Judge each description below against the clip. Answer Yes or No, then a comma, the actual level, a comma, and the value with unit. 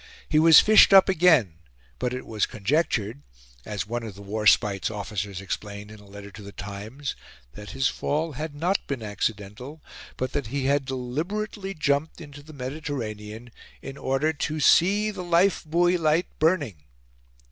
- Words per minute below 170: Yes, average, 160 wpm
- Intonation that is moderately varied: No, wide, 7.1 semitones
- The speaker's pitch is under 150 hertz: Yes, low, 135 Hz